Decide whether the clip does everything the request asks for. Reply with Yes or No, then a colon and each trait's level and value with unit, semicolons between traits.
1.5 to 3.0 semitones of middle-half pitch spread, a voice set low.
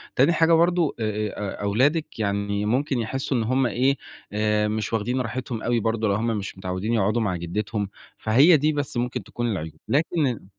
No: average, 4.2 semitones; low, 115 Hz